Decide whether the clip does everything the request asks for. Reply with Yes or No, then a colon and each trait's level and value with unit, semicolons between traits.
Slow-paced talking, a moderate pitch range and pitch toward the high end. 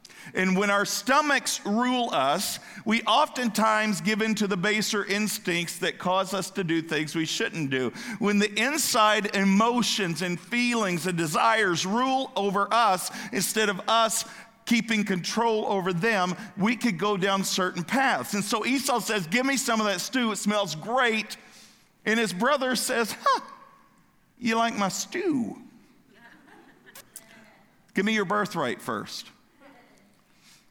No: average, 145 wpm; average, 3.4 semitones; high, 215 Hz